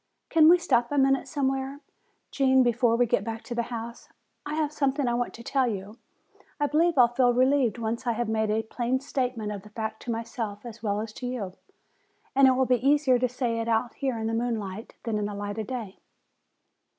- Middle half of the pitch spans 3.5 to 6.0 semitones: No, average, 3.1 semitones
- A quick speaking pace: Yes, fast, 225 wpm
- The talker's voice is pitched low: No, high, 240 Hz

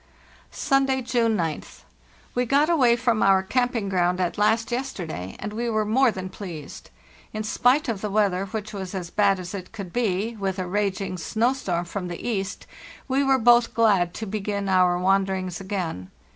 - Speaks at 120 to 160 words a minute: No, average, 180 wpm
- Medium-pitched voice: No, high, 205 Hz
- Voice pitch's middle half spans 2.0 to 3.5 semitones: No, average, 4.1 semitones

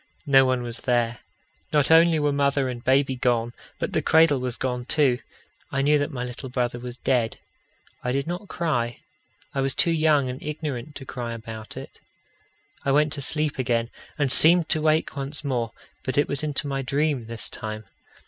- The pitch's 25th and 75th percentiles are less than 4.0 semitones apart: Yes, average, 3.3 semitones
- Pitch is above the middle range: No, low, 135 Hz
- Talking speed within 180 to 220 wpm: Yes, average, 190 wpm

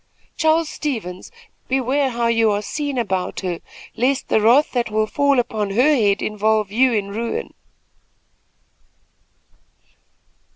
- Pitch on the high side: Yes, high, 230 Hz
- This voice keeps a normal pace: No, slow, 125 wpm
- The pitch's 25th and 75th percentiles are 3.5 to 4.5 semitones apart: Yes, average, 4.2 semitones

